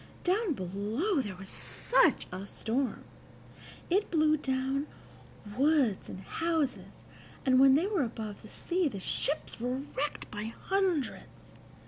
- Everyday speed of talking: No, slow, 130 wpm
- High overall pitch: Yes, very high, 270 Hz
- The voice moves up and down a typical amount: No, wide, 6.7 semitones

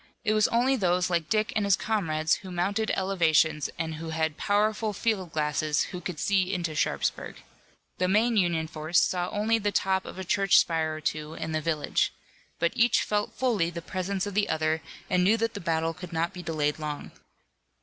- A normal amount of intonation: Yes, average, 4.3 semitones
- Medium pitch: Yes, medium, 180 Hz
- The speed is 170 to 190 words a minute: No, average, 200 wpm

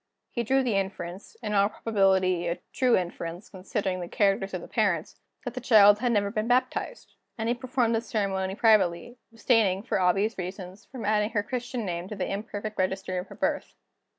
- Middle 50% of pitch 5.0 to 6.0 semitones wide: No, average, 3.4 semitones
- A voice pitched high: Yes, high, 205 Hz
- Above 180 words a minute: Yes, average, 190 wpm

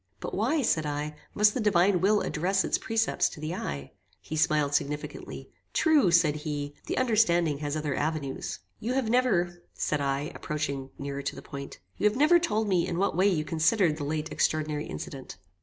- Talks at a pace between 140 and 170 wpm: No, average, 190 wpm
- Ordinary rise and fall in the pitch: No, wide, 5.9 semitones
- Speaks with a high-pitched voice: No, medium, 160 Hz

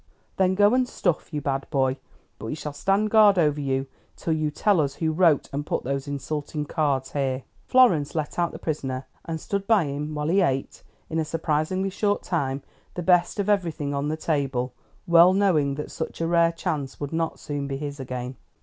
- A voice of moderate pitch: Yes, medium, 155 Hz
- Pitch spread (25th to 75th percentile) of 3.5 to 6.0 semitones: Yes, average, 3.9 semitones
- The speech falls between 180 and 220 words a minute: Yes, fast, 205 wpm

